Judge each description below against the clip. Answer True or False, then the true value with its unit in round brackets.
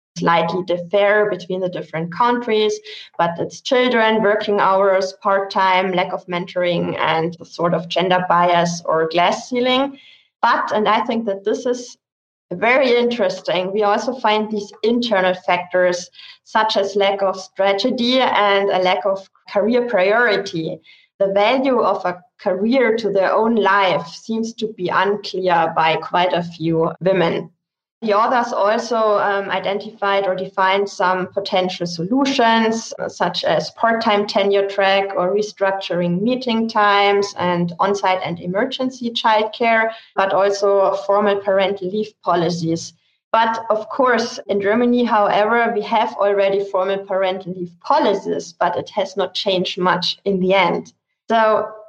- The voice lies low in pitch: False (200 Hz)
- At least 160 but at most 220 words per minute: False (140 wpm)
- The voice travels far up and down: False (3.2 semitones)